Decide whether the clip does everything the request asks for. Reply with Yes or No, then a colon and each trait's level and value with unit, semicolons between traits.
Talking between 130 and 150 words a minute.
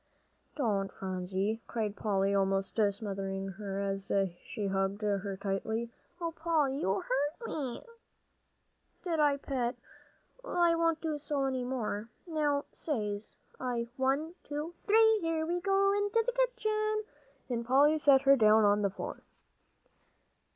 Yes: average, 145 wpm